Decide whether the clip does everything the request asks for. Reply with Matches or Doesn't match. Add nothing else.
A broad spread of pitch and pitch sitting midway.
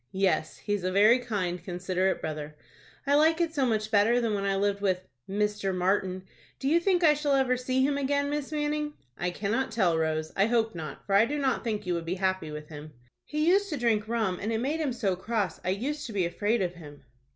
Doesn't match